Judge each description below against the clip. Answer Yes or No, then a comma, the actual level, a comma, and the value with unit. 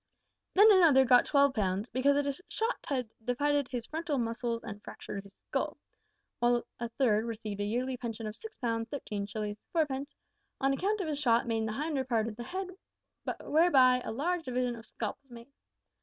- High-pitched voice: Yes, very high, 250 Hz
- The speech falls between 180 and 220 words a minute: Yes, average, 190 wpm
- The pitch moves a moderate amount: Yes, average, 4.0 semitones